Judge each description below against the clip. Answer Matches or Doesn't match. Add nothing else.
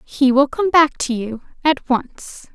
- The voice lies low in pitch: Doesn't match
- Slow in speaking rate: Doesn't match